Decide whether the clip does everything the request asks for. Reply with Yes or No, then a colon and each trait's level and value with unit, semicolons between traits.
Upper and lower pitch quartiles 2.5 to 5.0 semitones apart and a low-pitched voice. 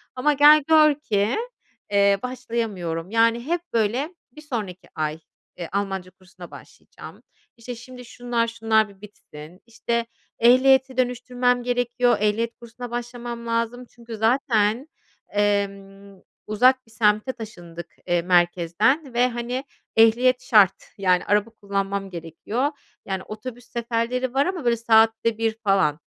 No: average, 3.7 semitones; high, 230 Hz